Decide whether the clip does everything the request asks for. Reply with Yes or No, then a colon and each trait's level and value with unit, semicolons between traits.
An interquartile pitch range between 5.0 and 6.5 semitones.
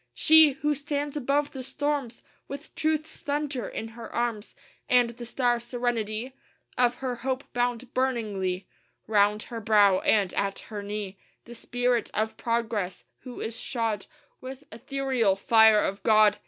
No: average, 3.7 semitones